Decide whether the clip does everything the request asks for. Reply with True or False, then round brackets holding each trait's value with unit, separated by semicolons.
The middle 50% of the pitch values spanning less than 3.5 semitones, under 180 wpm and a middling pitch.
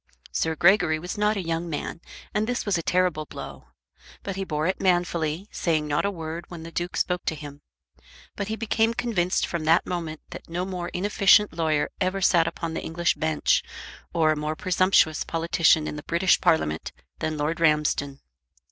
False (2.8 semitones; 185 wpm; 170 Hz)